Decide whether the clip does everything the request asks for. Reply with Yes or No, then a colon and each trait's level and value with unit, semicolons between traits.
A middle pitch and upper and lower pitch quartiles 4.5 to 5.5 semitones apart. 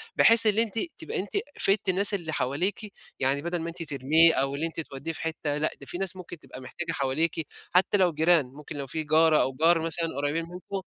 No: medium, 165 Hz; average, 3.7 semitones